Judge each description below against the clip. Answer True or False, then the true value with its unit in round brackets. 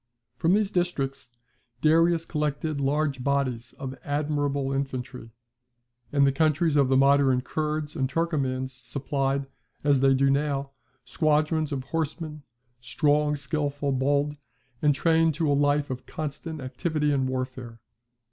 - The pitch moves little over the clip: True (2.2 semitones)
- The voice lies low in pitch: False (145 Hz)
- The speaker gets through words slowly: True (130 wpm)